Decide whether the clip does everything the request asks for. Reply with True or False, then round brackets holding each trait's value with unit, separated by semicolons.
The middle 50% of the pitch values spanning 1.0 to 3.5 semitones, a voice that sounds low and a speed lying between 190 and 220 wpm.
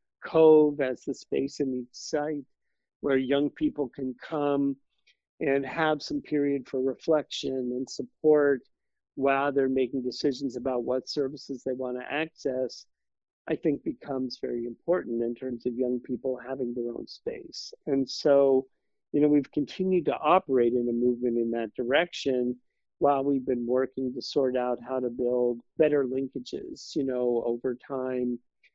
False (2.4 semitones; 130 Hz; 155 wpm)